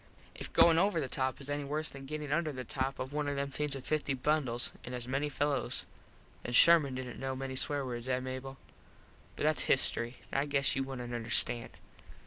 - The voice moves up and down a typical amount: No, narrow, 2.2 semitones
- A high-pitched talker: No, low, 135 Hz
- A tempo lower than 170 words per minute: No, fast, 205 wpm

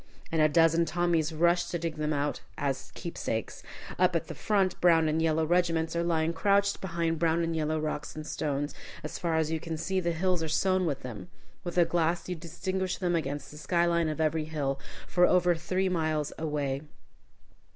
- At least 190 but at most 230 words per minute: Yes, average, 200 wpm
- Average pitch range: No, narrow, 2.1 semitones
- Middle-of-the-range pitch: Yes, medium, 165 Hz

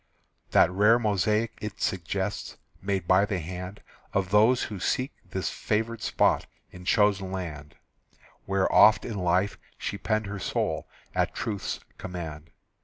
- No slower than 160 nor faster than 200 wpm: No, average, 140 wpm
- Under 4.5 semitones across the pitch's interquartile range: Yes, narrow, 2.6 semitones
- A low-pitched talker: Yes, low, 100 Hz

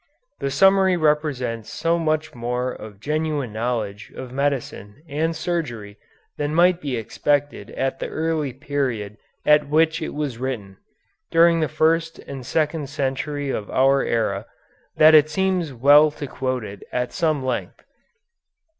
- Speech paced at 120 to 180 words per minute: Yes, average, 145 wpm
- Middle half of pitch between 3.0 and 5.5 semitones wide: Yes, average, 4.2 semitones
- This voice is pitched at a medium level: Yes, medium, 145 Hz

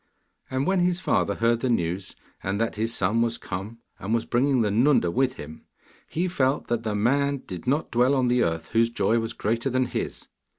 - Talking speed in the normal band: No, fast, 210 wpm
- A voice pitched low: Yes, low, 115 Hz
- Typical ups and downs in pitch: Yes, average, 3.6 semitones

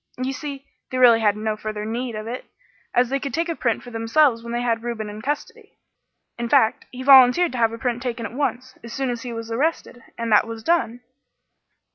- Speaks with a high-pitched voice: Yes, high, 240 Hz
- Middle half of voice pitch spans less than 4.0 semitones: Yes, average, 2.7 semitones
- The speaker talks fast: Yes, fast, 225 wpm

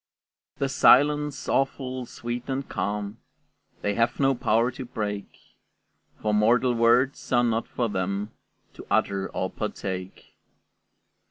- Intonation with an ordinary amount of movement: Yes, average, 3.9 semitones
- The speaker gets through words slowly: Yes, slow, 120 wpm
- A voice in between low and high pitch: No, low, 115 Hz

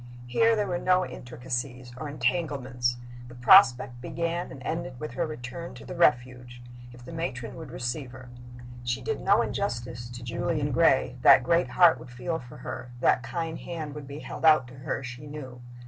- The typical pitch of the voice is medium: No, low, 130 Hz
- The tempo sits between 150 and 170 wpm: No, average, 185 wpm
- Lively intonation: No, average, 4.8 semitones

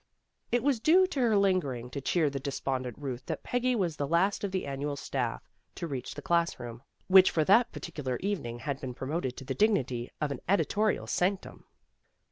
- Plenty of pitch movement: Yes, wide, 7.1 semitones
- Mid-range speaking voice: Yes, medium, 155 Hz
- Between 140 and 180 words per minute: No, average, 200 wpm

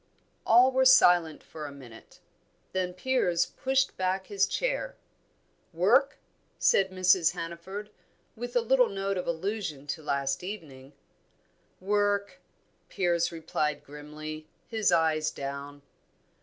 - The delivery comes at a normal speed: No, slow, 115 wpm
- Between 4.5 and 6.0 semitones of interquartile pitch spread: Yes, average, 5.2 semitones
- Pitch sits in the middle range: Yes, medium, 180 Hz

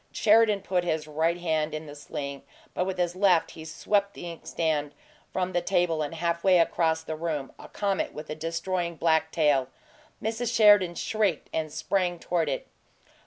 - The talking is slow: No, average, 175 wpm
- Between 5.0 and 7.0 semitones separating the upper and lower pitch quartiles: No, average, 2.9 semitones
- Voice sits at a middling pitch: Yes, medium, 170 Hz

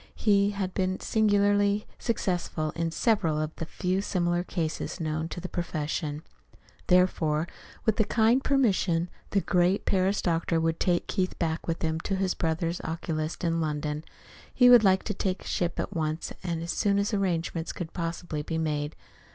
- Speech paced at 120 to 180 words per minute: Yes, average, 165 wpm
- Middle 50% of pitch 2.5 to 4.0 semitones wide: Yes, average, 3.4 semitones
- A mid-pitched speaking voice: Yes, medium, 175 Hz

